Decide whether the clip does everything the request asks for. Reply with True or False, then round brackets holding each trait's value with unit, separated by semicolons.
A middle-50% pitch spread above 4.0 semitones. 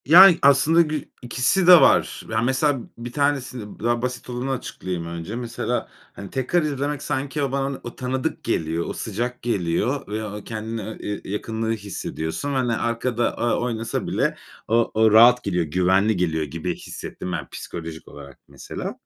True (4.8 semitones)